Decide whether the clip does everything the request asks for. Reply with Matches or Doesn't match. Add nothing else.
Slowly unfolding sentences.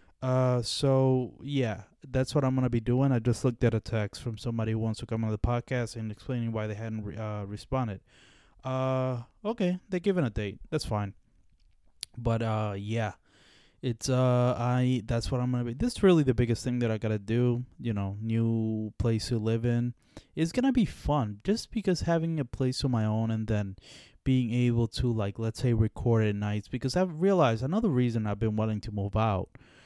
Doesn't match